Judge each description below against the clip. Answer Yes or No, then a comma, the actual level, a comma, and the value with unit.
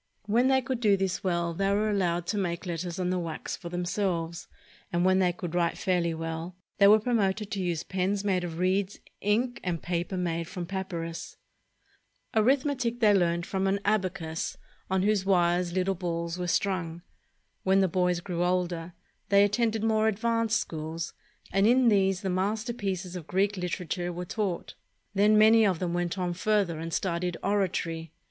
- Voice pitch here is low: No, medium, 185 Hz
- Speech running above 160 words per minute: Yes, average, 175 wpm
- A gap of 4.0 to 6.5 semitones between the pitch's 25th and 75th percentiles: No, average, 2.9 semitones